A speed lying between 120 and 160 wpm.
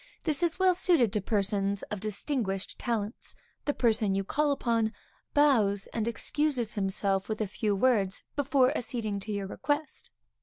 Yes: average, 150 wpm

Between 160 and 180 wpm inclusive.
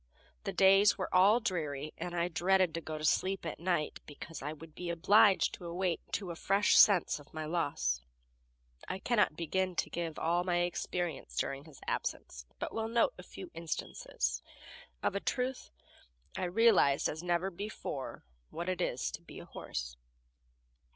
Yes: average, 170 wpm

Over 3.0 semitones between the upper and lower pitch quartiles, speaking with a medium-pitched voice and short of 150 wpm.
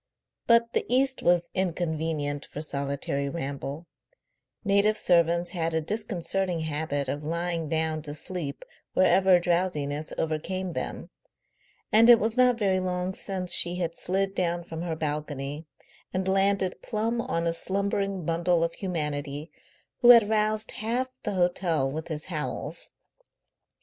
Yes: average, 3.7 semitones; medium, 175 Hz; average, 140 wpm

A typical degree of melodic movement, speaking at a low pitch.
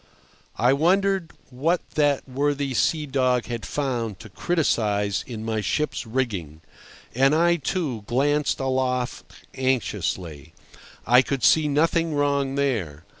Yes: average, 4.5 semitones; low, 130 Hz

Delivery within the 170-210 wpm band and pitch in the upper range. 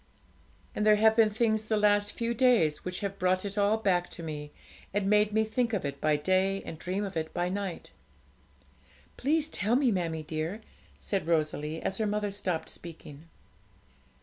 Yes: average, 180 wpm; high, 195 Hz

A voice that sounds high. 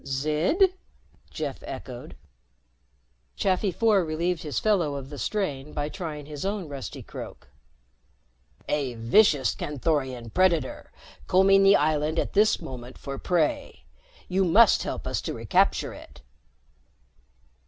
No: medium, 155 Hz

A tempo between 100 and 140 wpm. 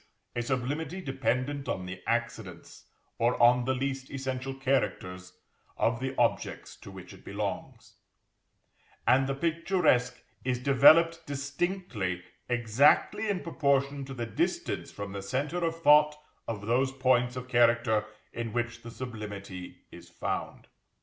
Yes: slow, 135 wpm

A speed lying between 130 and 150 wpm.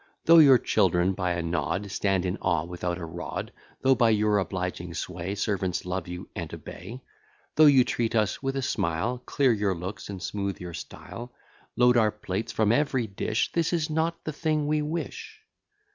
No: average, 185 wpm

